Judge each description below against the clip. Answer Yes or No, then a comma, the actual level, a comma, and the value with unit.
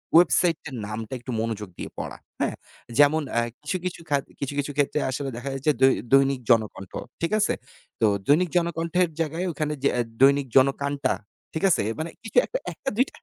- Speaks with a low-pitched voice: No, medium, 145 Hz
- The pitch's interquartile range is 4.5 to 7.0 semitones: No, average, 3.8 semitones